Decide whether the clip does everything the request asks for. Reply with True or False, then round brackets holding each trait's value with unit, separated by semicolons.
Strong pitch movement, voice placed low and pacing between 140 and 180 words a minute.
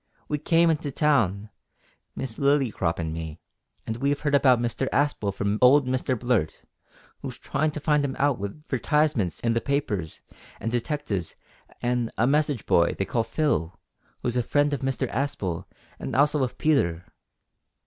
True (5.7 semitones; 130 Hz; 165 wpm)